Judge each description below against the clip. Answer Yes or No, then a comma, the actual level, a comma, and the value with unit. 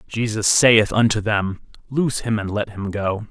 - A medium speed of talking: Yes, average, 180 wpm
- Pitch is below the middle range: Yes, low, 110 Hz